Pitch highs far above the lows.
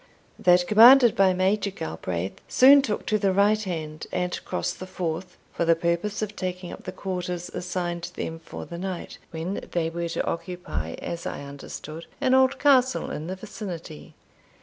No: average, 3.5 semitones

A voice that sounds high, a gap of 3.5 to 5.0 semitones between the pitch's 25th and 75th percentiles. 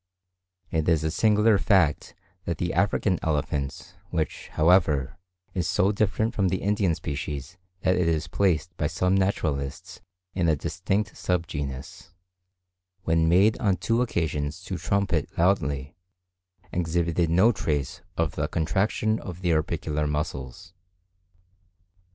No: very low, 85 Hz; average, 3.9 semitones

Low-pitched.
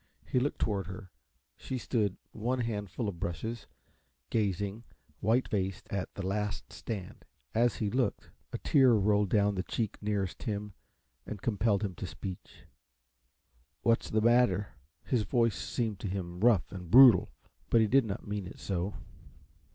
Yes: low, 105 Hz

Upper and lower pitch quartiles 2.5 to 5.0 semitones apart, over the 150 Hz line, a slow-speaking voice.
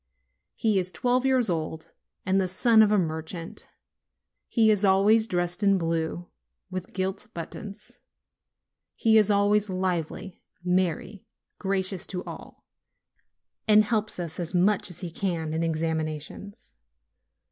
Yes: average, 3.7 semitones; medium, 185 Hz; slow, 130 wpm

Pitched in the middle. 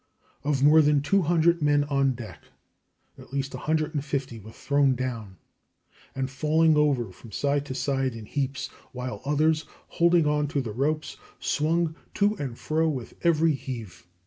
Yes: medium, 145 Hz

